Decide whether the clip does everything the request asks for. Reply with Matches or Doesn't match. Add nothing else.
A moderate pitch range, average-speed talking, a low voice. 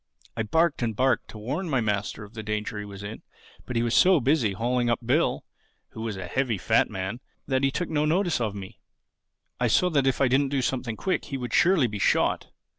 Doesn't match